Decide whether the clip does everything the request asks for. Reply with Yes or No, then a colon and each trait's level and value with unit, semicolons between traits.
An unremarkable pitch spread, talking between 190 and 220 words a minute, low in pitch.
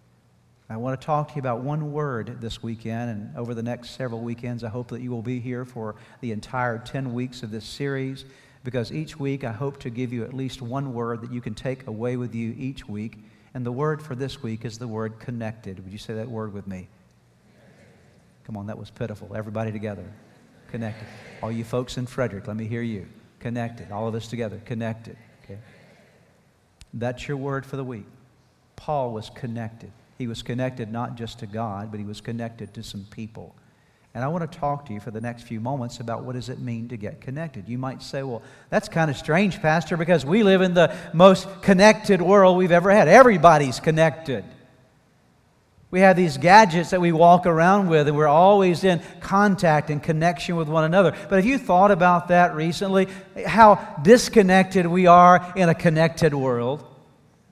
No: wide, 6.1 semitones; average, 200 wpm; low, 125 Hz